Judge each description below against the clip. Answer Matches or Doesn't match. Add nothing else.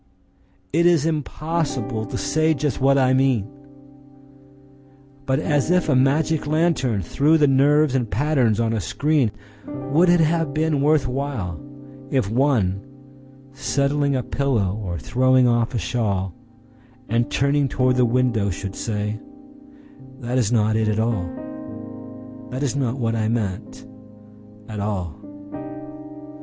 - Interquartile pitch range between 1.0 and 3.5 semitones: Doesn't match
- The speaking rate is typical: Doesn't match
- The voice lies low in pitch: Matches